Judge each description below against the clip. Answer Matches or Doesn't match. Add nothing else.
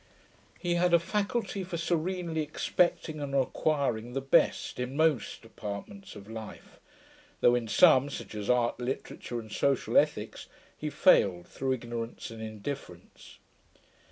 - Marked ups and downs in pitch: Matches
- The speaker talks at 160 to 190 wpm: Doesn't match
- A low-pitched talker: Matches